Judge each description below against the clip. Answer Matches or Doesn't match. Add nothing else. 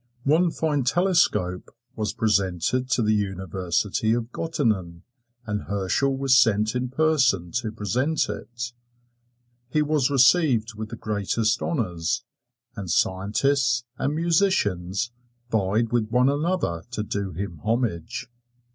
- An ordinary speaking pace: Doesn't match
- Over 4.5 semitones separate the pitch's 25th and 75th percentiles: Matches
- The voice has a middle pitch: Doesn't match